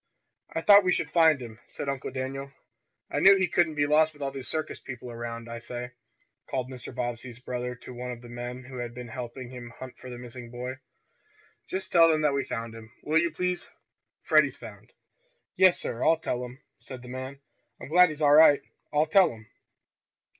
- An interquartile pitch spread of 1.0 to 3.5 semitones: No, average, 4.0 semitones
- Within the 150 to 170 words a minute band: No, fast, 205 wpm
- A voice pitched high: No, low, 130 Hz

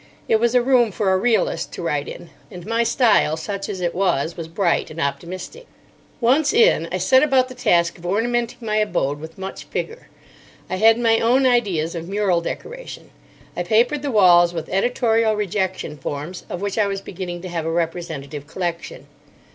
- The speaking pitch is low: No, high, 195 Hz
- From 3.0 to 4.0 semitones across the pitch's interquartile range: No, wide, 5.6 semitones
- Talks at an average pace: Yes, average, 185 wpm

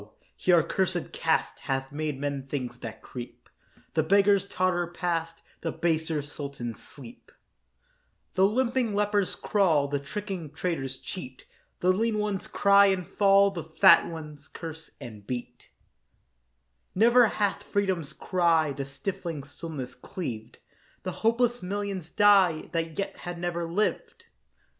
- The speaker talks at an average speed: No, slow, 130 wpm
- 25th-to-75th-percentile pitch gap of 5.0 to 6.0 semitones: Yes, wide, 5.4 semitones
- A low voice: No, medium, 170 Hz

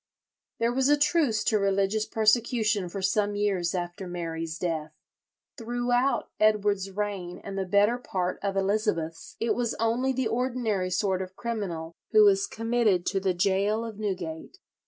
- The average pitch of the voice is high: Yes, high, 205 Hz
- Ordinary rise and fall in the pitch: Yes, average, 3.9 semitones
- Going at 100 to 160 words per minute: Yes, average, 155 wpm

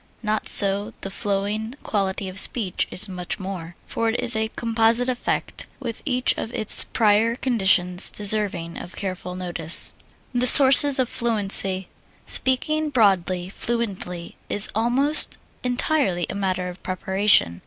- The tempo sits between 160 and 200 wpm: No, slow, 135 wpm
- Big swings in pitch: No, average, 4.2 semitones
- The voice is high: Yes, high, 205 Hz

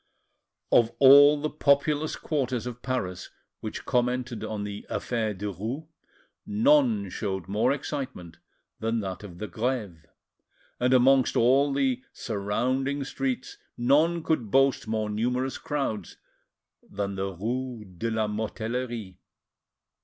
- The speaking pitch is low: Yes, low, 125 Hz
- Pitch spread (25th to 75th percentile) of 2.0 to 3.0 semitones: No, average, 4.3 semitones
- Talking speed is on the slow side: Yes, slow, 120 wpm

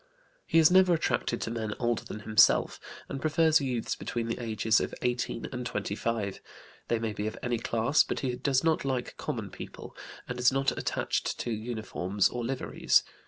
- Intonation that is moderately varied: Yes, average, 3.2 semitones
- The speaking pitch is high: No, low, 120 Hz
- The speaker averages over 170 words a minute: Yes, average, 180 wpm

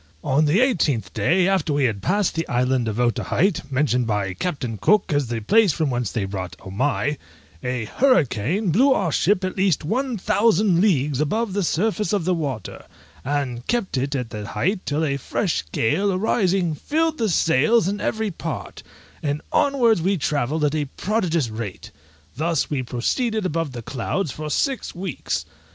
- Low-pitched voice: No, medium, 155 Hz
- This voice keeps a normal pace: Yes, average, 170 wpm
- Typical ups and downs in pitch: No, wide, 7.6 semitones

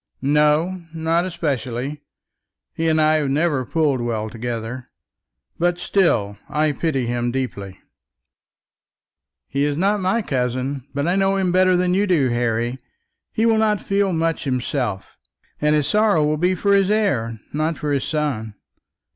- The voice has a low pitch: No, medium, 150 Hz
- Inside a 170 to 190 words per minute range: No, average, 155 wpm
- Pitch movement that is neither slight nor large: No, wide, 6.2 semitones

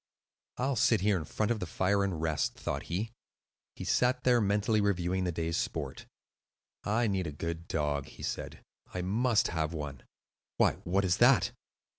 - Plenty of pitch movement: No, average, 4.5 semitones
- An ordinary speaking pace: Yes, average, 175 wpm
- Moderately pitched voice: No, very low, 95 Hz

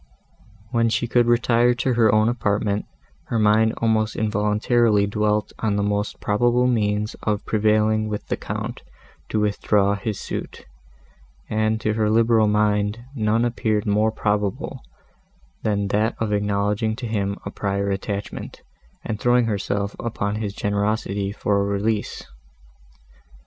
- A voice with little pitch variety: Yes, narrow, 1.5 semitones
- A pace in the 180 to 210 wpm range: No, average, 140 wpm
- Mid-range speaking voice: No, low, 105 Hz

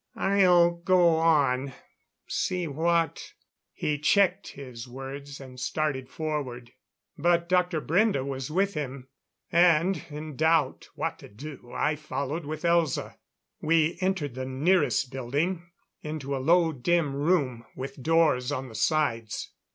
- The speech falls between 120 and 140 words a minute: Yes, slow, 135 wpm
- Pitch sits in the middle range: Yes, medium, 150 Hz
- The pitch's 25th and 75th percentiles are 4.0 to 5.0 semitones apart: Yes, average, 4.3 semitones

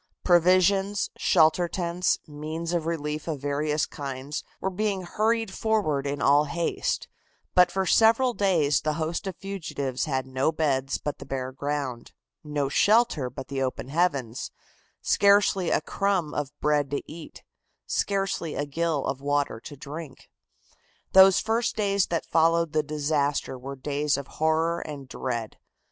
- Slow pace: No, average, 150 wpm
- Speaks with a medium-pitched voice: Yes, medium, 155 Hz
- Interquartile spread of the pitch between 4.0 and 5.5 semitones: Yes, average, 4.4 semitones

